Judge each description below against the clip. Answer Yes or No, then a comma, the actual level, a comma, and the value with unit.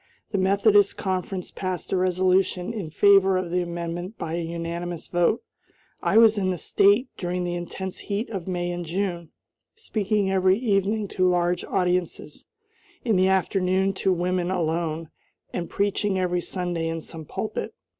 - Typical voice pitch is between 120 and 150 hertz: No, medium, 185 Hz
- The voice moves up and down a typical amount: No, narrow, 2.0 semitones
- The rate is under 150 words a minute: No, average, 155 wpm